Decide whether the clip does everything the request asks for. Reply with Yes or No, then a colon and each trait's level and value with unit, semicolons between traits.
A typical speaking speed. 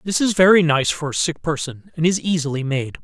No: fast, 235 wpm